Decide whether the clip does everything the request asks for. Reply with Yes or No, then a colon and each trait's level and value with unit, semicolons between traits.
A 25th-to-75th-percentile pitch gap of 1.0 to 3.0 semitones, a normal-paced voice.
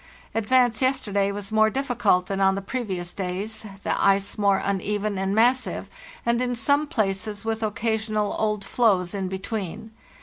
Yes: narrow, 2.6 semitones; average, 160 wpm